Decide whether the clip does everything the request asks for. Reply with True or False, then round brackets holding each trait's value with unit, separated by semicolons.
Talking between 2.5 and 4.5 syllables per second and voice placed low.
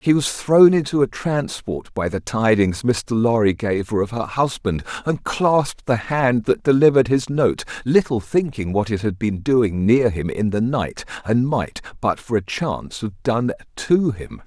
True (4.4 syllables/s; 120 Hz)